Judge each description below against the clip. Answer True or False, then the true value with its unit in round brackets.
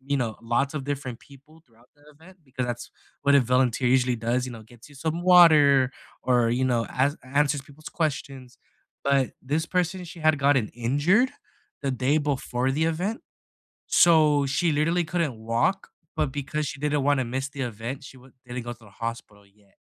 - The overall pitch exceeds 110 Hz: True (135 Hz)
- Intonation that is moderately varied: True (3.7 semitones)